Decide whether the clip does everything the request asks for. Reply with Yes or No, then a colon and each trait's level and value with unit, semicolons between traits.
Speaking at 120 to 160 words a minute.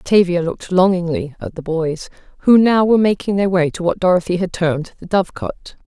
No: fast, 205 wpm